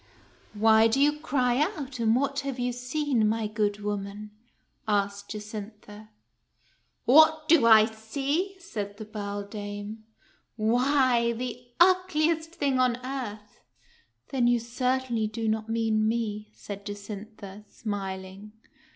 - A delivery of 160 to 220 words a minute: No, slow, 135 wpm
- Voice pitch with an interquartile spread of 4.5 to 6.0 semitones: No, average, 3.8 semitones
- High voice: Yes, high, 225 Hz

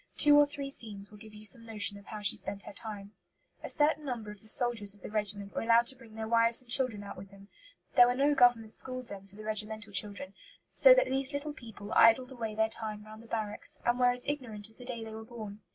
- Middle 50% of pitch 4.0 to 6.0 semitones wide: No, average, 3.0 semitones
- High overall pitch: Yes, high, 220 Hz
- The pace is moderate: No, fast, 255 wpm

